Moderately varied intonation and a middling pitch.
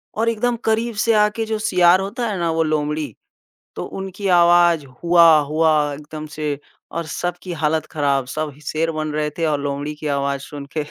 Yes: average, 3.5 semitones; medium, 160 Hz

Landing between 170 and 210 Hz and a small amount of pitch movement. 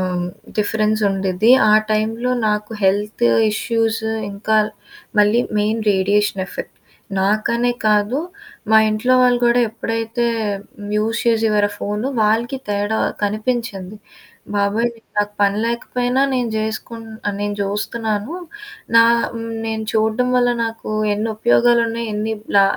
No: high, 220 Hz; narrow, 2.0 semitones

